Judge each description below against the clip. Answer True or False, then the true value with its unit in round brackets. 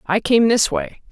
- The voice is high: True (220 Hz)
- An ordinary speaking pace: False (215 wpm)